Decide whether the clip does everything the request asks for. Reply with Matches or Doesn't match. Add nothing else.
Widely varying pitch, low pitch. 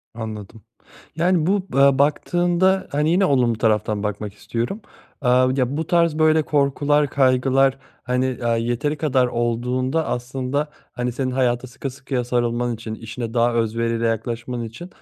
Doesn't match